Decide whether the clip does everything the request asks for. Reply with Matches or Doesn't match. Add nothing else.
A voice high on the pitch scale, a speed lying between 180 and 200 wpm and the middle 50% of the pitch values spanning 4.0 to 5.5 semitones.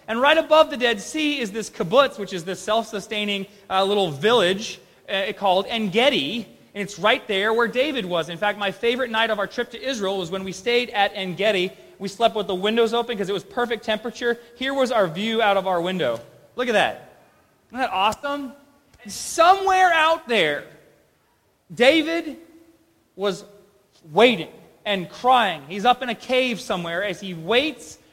Matches